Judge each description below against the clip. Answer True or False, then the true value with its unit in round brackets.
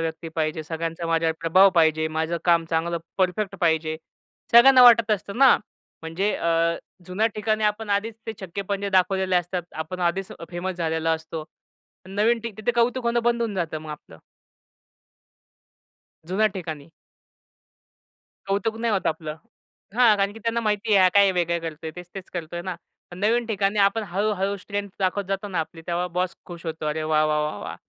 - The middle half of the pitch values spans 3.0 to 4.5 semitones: True (4.2 semitones)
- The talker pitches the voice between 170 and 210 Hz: True (185 Hz)